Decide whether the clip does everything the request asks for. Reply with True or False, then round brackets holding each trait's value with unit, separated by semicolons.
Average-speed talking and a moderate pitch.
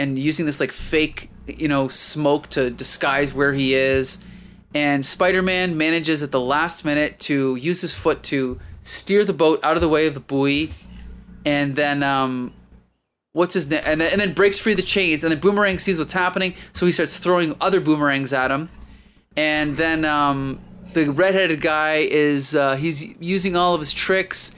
True (185 wpm; 155 Hz)